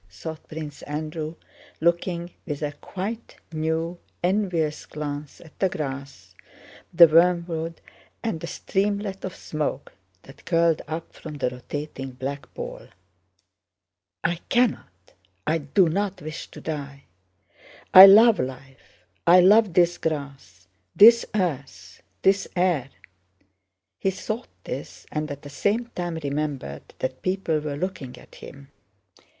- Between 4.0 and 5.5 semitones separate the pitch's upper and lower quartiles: Yes, average, 4.5 semitones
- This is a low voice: No, medium, 160 Hz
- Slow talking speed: Yes, slow, 125 wpm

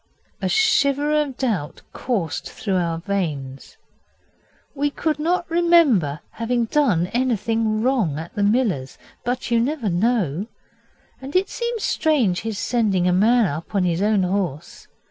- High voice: Yes, high, 225 Hz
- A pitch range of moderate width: No, wide, 7.2 semitones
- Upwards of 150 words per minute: No, average, 145 wpm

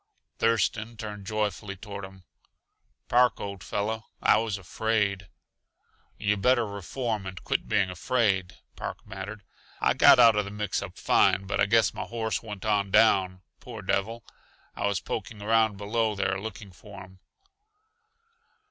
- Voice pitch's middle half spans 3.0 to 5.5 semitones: No, narrow, 2.4 semitones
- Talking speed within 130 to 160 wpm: Yes, average, 150 wpm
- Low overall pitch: Yes, low, 105 Hz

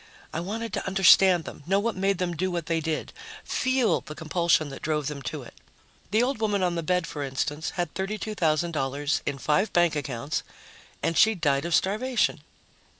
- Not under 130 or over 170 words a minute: No, average, 185 wpm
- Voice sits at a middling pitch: Yes, medium, 175 Hz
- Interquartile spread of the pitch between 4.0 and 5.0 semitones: Yes, average, 4.3 semitones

